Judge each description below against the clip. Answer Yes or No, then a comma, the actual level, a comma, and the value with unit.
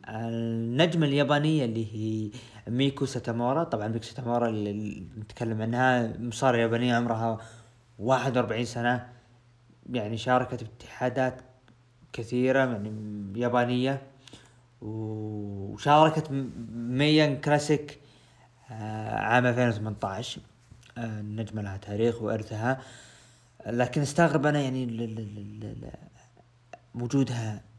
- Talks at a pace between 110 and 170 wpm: No, average, 80 wpm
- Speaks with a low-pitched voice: Yes, low, 120 Hz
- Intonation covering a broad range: No, narrow, 2.4 semitones